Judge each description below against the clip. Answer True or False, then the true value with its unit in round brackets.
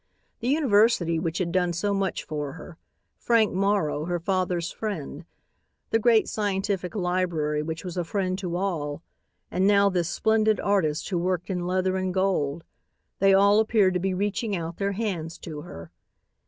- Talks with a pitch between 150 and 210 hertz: True (185 Hz)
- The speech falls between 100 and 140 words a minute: False (170 wpm)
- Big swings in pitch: False (3.1 semitones)